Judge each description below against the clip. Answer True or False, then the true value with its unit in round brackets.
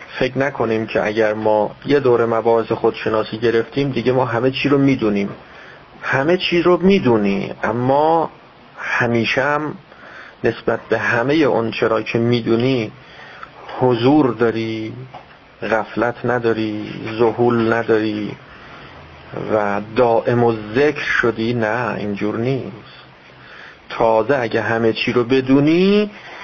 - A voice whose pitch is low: True (115 Hz)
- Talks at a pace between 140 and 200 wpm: False (115 wpm)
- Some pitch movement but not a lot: True (3.0 semitones)